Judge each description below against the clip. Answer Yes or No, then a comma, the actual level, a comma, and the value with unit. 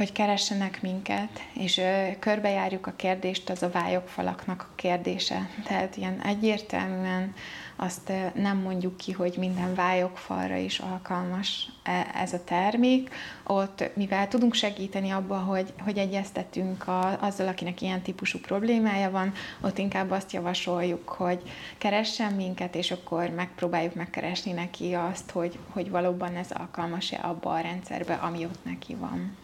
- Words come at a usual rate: Yes, average, 135 wpm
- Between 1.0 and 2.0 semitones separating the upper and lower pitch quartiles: Yes, narrow, 1.7 semitones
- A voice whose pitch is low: No, medium, 185 Hz